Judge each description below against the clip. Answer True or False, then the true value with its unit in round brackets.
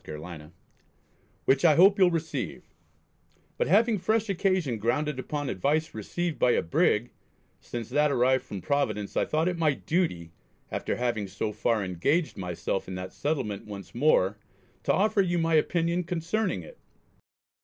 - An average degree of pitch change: False (8.7 semitones)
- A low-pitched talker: False (145 Hz)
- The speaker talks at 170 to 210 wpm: False (155 wpm)